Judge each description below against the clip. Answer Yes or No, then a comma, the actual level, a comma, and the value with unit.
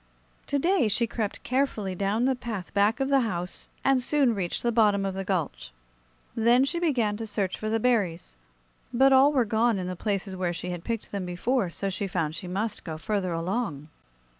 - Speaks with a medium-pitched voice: No, high, 210 Hz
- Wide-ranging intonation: No, average, 4.8 semitones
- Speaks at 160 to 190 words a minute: No, fast, 205 wpm